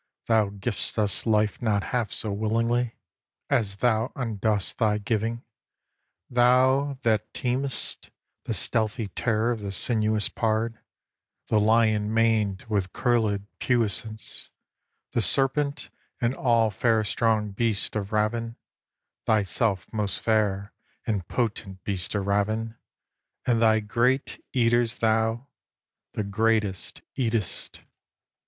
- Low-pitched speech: Yes, low, 110 Hz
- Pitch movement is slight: Yes, narrow, 2.0 semitones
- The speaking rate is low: Yes, slow, 115 wpm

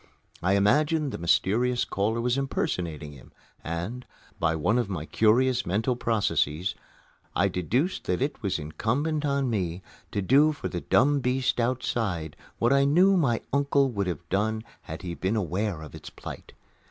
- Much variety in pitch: Yes, wide, 6.5 semitones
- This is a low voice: Yes, low, 110 Hz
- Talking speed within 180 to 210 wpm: No, average, 165 wpm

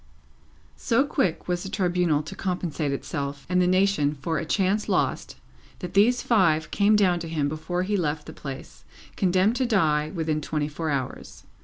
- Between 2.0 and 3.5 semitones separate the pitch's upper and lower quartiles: No, average, 4.1 semitones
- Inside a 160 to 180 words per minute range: Yes, average, 175 wpm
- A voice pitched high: No, medium, 175 Hz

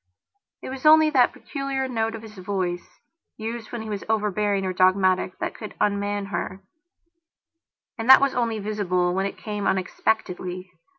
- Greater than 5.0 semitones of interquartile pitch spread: No, average, 3.4 semitones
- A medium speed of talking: Yes, average, 155 wpm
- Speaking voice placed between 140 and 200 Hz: No, high, 210 Hz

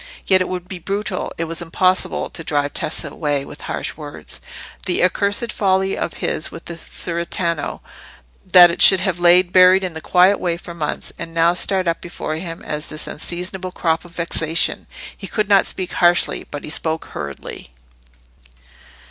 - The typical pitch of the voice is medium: Yes, medium, 175 Hz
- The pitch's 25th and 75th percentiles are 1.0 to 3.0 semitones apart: Yes, narrow, 2.4 semitones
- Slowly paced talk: No, average, 165 wpm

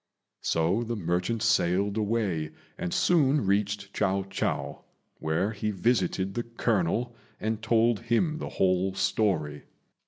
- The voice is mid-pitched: No, low, 105 Hz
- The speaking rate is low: Yes, slow, 125 wpm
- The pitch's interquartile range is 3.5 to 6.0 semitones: Yes, average, 3.8 semitones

